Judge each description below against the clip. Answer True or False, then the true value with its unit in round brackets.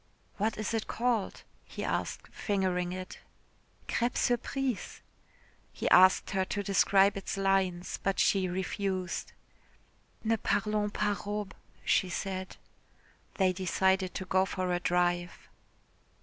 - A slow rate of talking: True (120 wpm)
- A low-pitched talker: False (190 Hz)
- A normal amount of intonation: False (2.0 semitones)